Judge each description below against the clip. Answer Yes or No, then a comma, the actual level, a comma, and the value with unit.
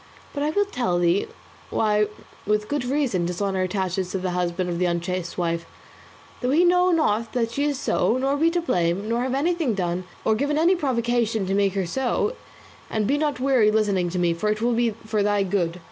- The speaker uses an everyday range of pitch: No, wide, 6.7 semitones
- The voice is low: No, high, 215 Hz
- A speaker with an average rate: No, fast, 215 wpm